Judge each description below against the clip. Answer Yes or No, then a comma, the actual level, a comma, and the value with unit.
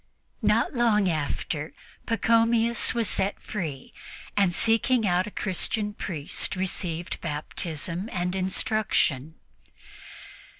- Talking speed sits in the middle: No, slow, 95 wpm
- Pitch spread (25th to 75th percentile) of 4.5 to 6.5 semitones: Yes, average, 4.9 semitones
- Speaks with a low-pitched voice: No, high, 190 Hz